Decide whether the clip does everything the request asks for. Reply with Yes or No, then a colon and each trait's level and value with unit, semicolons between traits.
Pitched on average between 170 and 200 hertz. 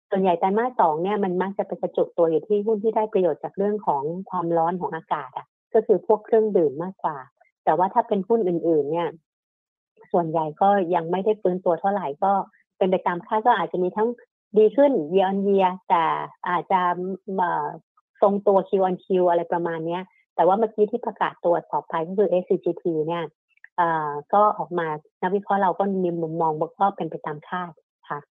Yes: medium, 185 Hz